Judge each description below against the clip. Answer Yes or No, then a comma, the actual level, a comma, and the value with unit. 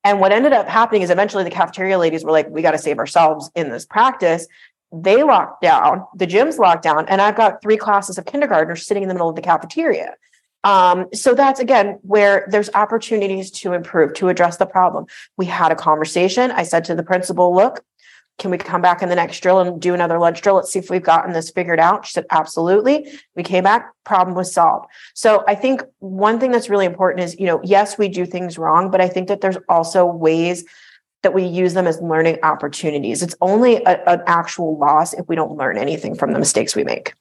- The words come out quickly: Yes, fast, 225 wpm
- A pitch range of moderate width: Yes, average, 3.1 semitones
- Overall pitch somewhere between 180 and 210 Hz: Yes, medium, 185 Hz